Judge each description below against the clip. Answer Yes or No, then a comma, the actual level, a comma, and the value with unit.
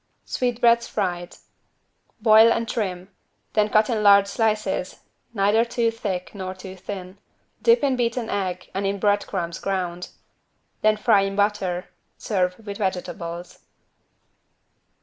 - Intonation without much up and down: No, average, 3.1 semitones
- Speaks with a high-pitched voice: Yes, high, 200 Hz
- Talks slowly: Yes, slow, 130 wpm